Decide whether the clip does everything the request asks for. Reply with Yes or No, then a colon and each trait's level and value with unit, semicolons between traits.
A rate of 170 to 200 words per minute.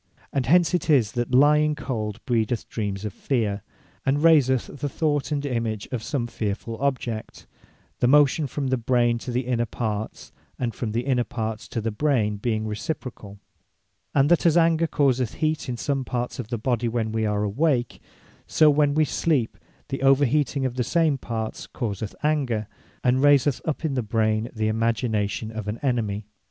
Yes: average, 180 wpm